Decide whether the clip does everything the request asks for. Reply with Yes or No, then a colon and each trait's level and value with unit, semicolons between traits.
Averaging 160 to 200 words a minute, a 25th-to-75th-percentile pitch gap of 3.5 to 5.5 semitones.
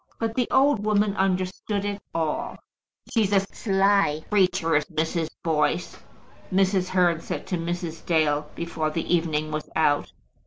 No: average, 145 wpm; average, 3.9 semitones